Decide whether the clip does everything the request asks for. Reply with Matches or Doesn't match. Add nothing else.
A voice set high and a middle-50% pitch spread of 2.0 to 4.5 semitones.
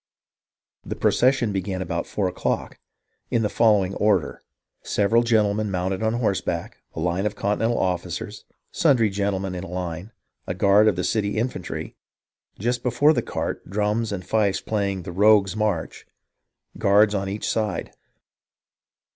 Doesn't match